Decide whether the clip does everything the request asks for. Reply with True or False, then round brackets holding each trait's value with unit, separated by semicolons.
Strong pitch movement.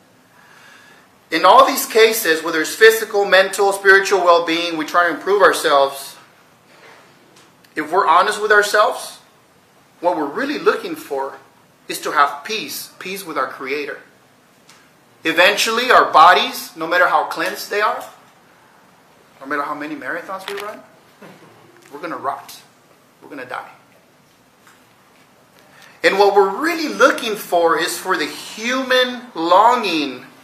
True (6.1 semitones)